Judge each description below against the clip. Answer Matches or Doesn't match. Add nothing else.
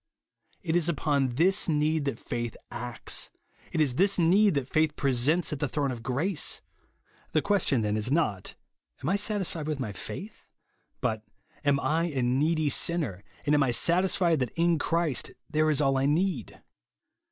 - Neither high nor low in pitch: Matches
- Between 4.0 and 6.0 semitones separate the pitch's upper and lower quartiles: Matches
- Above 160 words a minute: Matches